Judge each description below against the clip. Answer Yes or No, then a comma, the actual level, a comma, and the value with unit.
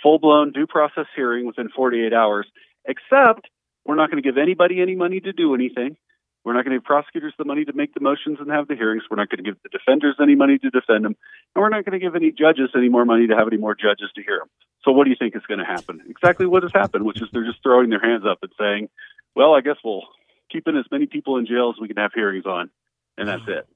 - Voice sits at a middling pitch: Yes, medium, 150 Hz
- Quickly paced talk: Yes, fast, 280 wpm